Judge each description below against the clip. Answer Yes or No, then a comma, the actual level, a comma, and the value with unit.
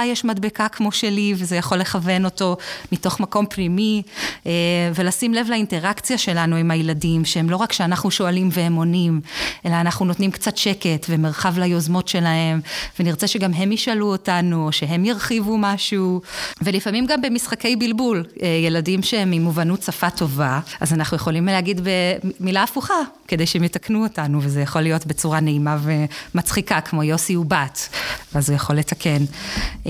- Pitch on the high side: No, medium, 180 Hz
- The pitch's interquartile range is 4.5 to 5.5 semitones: No, average, 3.7 semitones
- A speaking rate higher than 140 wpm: Yes, fast, 150 wpm